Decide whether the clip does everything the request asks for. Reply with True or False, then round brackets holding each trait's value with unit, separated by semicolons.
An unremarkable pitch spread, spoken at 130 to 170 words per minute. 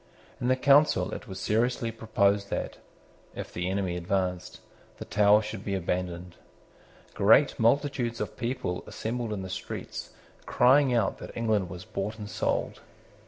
True (4.0 semitones; 150 wpm)